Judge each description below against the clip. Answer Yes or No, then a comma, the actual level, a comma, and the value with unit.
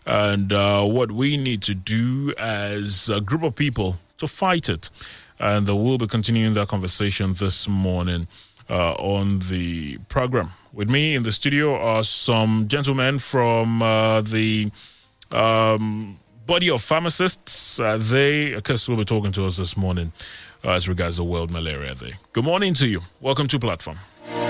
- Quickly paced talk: No, average, 165 wpm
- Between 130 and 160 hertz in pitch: No, low, 110 Hz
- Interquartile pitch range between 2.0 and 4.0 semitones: No, average, 4.4 semitones